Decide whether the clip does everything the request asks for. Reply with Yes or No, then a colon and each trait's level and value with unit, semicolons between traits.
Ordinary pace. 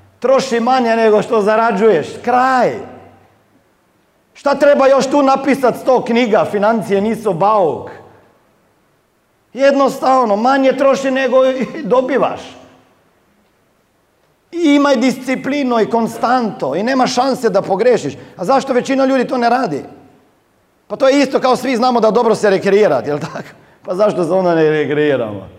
Yes: average, 135 wpm